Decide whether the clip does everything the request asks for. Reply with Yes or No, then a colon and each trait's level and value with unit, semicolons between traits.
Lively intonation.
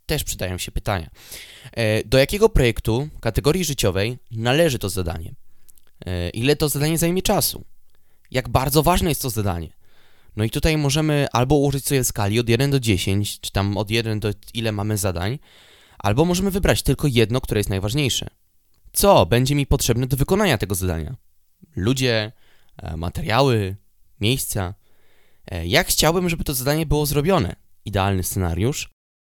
Yes: wide, 6.3 semitones